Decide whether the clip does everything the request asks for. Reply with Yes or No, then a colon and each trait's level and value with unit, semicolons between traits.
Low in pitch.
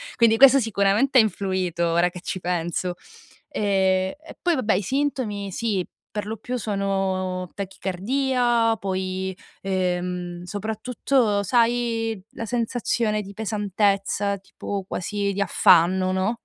No: high, 200 Hz